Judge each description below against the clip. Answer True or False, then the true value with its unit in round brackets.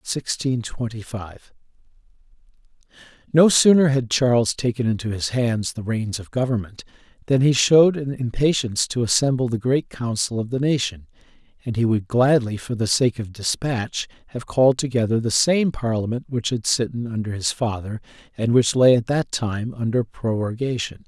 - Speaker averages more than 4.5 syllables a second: True (4.9 syllables/s)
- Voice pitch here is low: True (120 Hz)